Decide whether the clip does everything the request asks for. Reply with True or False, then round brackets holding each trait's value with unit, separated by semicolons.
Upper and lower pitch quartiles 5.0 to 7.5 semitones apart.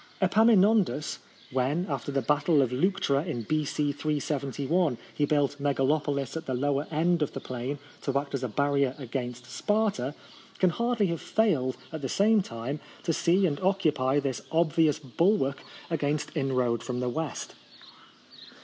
False (4.0 semitones)